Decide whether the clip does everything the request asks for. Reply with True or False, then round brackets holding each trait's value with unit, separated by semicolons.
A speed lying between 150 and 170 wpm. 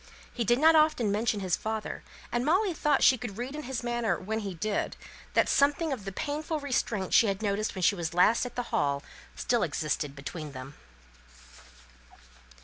False (185 wpm)